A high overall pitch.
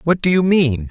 No: medium, 155 Hz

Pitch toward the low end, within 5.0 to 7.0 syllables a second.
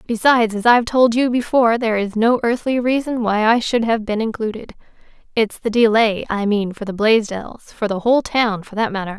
No: high, 225 Hz; 5.5 syllables/s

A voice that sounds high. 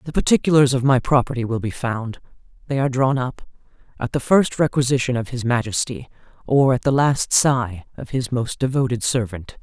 No: low, 125 Hz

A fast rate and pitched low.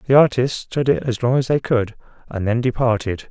Yes: fast, 220 wpm; low, 120 Hz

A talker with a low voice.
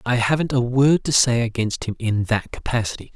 Yes: low, 120 Hz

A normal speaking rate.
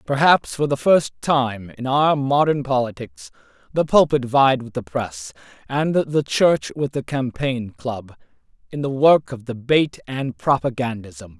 Yes: average, 155 wpm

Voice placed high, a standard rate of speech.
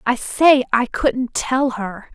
Yes: high, 245 Hz; average, 170 wpm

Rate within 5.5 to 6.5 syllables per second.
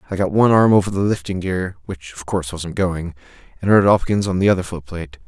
Yes: 5.6 syllables/s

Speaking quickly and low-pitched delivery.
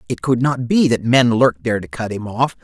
Yes: fast, 275 wpm; low, 115 Hz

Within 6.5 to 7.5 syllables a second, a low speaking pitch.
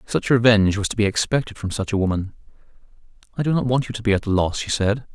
Yes: 6.8 syllables/s; low, 110 Hz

